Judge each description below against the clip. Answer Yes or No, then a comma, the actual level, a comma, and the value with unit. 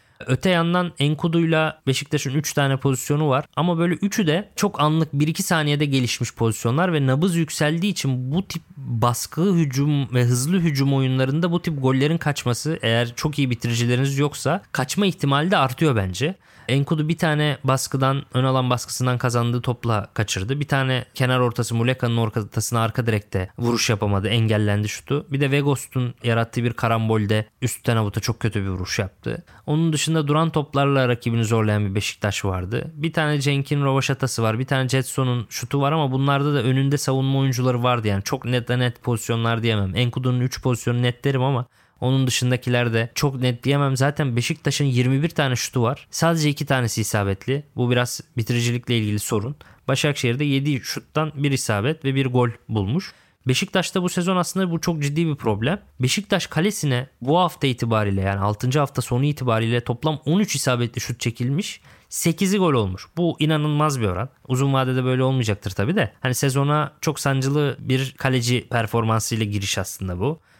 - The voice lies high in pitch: No, low, 130 Hz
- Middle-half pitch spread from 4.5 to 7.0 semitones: No, average, 3.8 semitones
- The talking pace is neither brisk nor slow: No, fast, 165 wpm